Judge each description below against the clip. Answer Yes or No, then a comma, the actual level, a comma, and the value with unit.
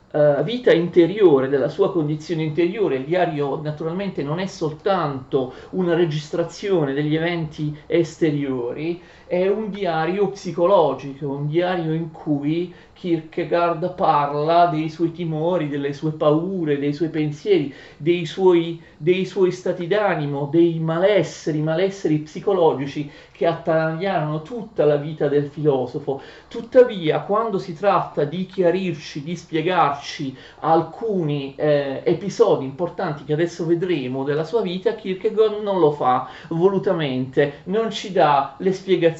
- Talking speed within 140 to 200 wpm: No, average, 125 wpm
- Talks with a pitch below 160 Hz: No, medium, 165 Hz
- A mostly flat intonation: No, average, 3.3 semitones